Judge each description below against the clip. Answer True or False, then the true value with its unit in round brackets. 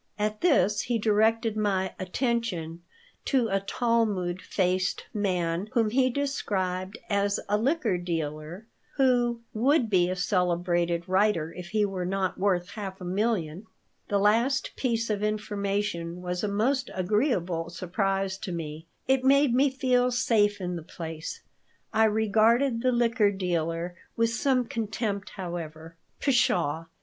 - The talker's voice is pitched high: True (205 Hz)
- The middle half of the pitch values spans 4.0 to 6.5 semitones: True (4.4 semitones)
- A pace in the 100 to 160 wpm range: True (140 wpm)